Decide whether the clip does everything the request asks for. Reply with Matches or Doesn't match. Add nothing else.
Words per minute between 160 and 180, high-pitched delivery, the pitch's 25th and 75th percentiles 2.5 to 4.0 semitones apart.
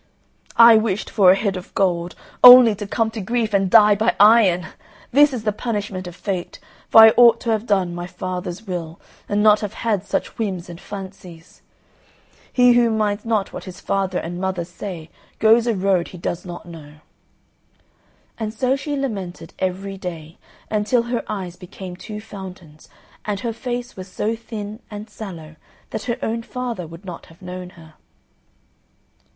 Matches